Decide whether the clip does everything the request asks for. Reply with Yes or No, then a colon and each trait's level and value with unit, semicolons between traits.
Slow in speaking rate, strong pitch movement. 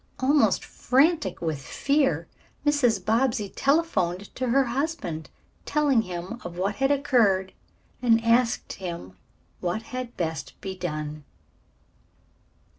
Yes: slow, 115 wpm; wide, 7.1 semitones